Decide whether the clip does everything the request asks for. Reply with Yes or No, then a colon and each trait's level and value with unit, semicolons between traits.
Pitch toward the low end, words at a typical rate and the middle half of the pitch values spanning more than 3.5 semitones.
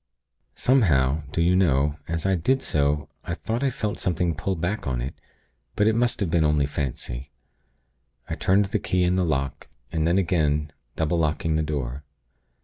Yes: very low, 80 Hz; average, 180 wpm; average, 4.5 semitones